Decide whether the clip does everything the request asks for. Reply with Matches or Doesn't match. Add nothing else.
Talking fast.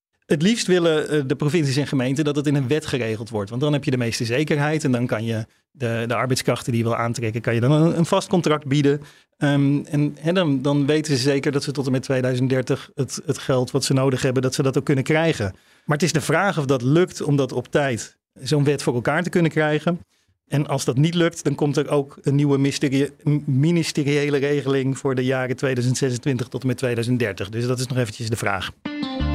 Matches